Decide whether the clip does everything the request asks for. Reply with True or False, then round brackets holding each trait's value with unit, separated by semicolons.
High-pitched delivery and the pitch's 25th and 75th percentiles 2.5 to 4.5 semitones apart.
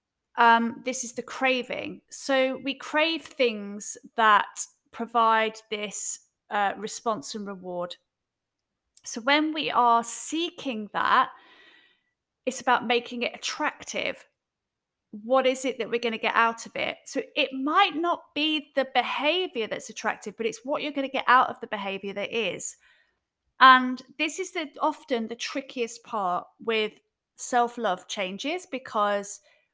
True (245 Hz; 3.9 semitones)